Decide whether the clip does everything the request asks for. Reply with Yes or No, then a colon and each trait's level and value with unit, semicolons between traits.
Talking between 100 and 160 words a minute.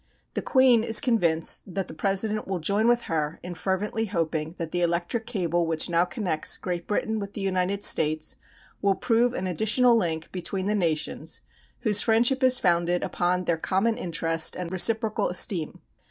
No: average, 170 wpm